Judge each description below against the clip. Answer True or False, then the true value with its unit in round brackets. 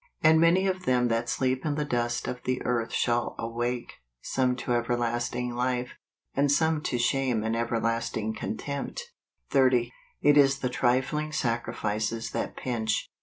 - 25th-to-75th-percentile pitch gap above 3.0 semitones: False (2.7 semitones)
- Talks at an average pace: True (155 wpm)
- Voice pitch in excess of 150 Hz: False (125 Hz)